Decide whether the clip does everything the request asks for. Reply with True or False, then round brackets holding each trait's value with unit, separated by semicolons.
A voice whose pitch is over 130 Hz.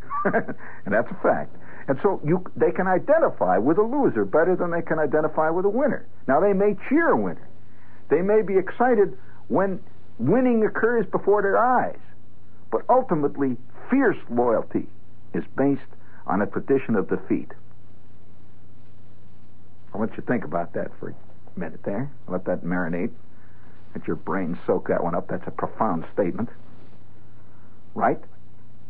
True (140 Hz)